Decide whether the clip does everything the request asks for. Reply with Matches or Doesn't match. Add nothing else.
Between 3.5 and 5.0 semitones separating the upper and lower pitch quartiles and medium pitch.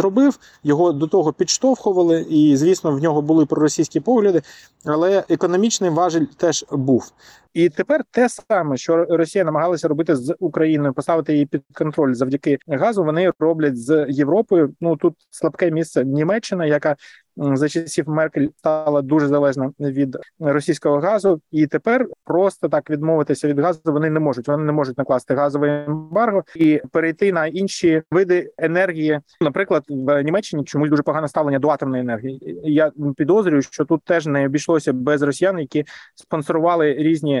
Doesn't match